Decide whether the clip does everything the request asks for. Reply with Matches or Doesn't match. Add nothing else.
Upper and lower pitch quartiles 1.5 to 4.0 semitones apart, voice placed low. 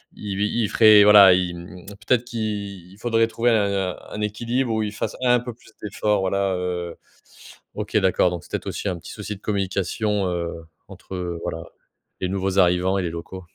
Matches